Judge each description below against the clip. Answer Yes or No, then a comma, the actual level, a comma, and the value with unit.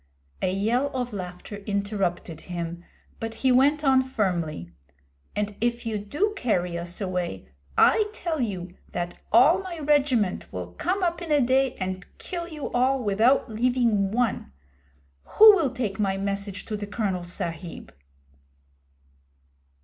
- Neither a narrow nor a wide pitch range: No, wide, 6.3 semitones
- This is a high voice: Yes, high, 215 Hz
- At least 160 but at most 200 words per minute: No, average, 140 wpm